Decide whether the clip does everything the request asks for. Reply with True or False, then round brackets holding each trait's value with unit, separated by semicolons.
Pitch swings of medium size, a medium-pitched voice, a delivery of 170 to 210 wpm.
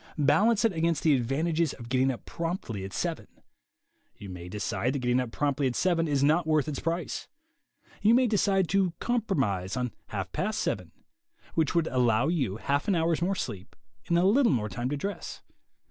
False (6.1 semitones; 150 Hz; 190 wpm)